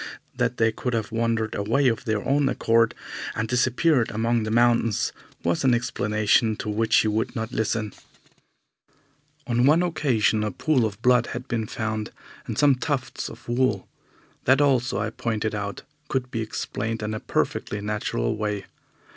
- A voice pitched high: No, low, 115 Hz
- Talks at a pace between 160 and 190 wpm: Yes, average, 165 wpm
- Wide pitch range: No, narrow, 2.5 semitones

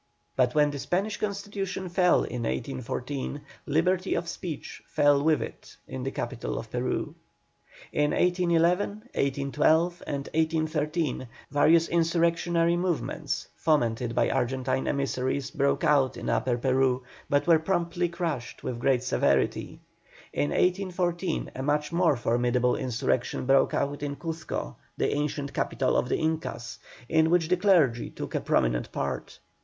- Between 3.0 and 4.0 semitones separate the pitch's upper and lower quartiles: No, average, 4.5 semitones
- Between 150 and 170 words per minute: No, average, 140 wpm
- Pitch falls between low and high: Yes, medium, 150 Hz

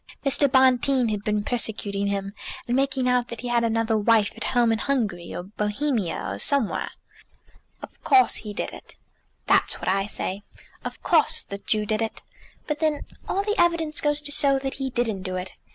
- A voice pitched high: Yes, high, 235 Hz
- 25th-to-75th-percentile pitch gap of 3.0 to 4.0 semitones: No, average, 5.0 semitones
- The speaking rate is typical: Yes, average, 190 wpm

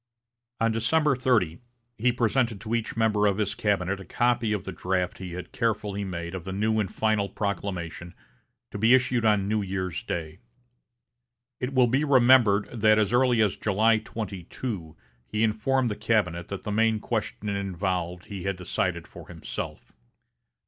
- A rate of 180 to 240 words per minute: No, average, 165 wpm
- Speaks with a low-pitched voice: Yes, low, 105 Hz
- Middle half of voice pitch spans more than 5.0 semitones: No, average, 3.3 semitones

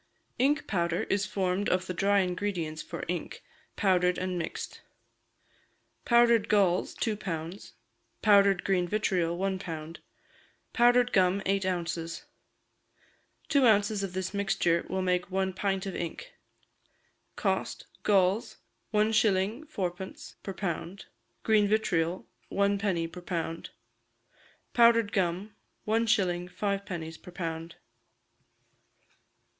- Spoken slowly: Yes, slow, 110 wpm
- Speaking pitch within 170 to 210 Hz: Yes, high, 190 Hz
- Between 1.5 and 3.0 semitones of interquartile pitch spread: Yes, narrow, 2.6 semitones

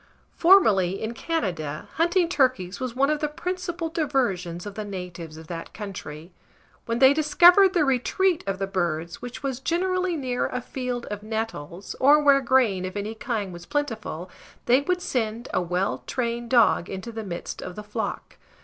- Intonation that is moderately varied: No, wide, 7.5 semitones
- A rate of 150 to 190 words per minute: Yes, average, 175 wpm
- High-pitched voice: Yes, high, 235 Hz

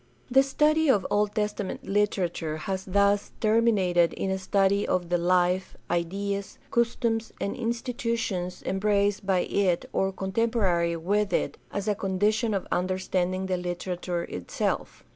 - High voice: Yes, high, 195 Hz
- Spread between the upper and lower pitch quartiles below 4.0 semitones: Yes, average, 2.7 semitones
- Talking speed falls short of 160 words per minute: Yes, average, 140 wpm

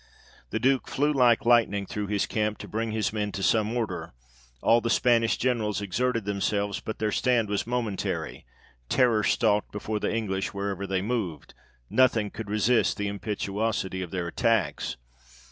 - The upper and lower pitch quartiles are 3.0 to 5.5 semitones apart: No, narrow, 2.5 semitones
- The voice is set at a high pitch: No, low, 105 Hz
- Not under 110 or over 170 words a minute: Yes, average, 160 wpm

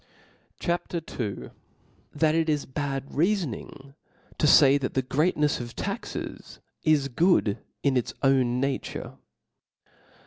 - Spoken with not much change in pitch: No, average, 3.1 semitones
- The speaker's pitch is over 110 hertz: Yes, medium, 140 Hz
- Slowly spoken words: Yes, slow, 125 wpm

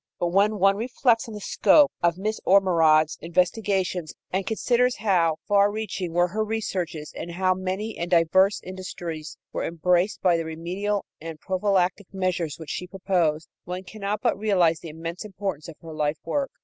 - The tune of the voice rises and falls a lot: No, average, 3.4 semitones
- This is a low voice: No, medium, 185 Hz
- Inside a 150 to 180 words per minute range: Yes, average, 170 wpm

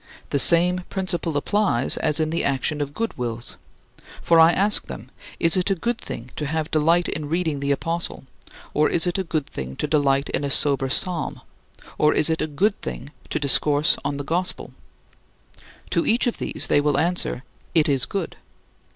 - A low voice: No, medium, 155 Hz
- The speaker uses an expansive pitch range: No, average, 3.6 semitones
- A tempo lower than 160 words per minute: No, average, 190 wpm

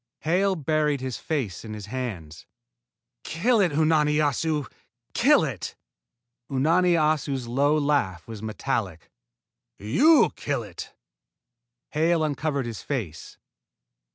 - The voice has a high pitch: No, medium, 145 Hz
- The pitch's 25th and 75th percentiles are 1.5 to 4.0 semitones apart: No, wide, 5.4 semitones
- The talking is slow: Yes, slow, 110 wpm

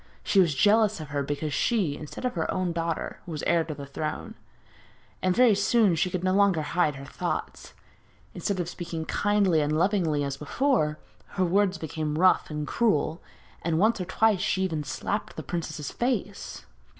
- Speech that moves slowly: No, average, 180 wpm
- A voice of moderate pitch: Yes, medium, 170 Hz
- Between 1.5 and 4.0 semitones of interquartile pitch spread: No, average, 4.7 semitones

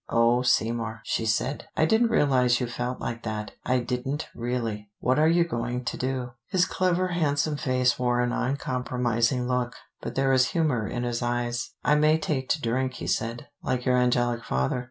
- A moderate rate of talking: Yes, average, 185 wpm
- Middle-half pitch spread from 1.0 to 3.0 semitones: Yes, narrow, 2.6 semitones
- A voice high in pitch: No, low, 125 Hz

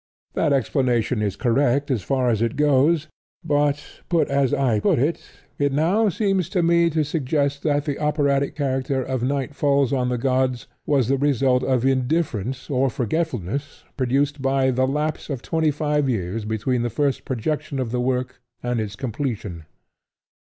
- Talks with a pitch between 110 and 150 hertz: Yes, low, 135 Hz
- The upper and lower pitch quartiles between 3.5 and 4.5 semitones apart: No, average, 2.9 semitones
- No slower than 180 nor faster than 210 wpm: No, average, 165 wpm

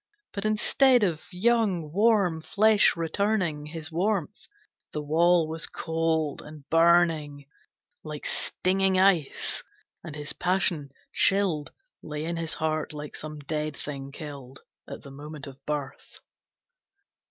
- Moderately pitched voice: Yes, medium, 160 Hz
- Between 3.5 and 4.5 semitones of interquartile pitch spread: Yes, average, 3.8 semitones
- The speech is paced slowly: Yes, slow, 125 wpm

